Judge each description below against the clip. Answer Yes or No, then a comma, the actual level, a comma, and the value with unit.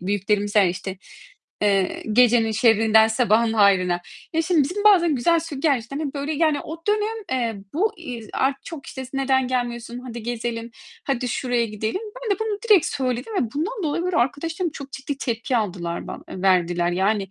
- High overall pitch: Yes, high, 245 Hz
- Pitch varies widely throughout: Yes, wide, 6.2 semitones